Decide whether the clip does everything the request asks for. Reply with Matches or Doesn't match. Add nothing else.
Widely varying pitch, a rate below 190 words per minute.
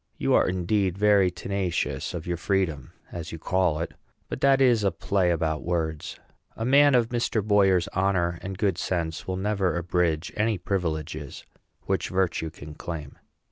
Doesn't match